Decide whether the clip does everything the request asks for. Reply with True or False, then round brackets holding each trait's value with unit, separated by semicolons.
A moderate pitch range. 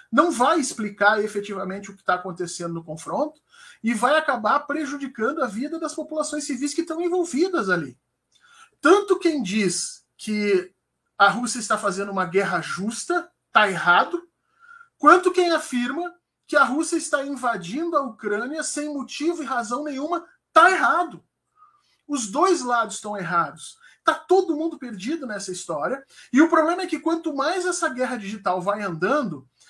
False (8.0 semitones)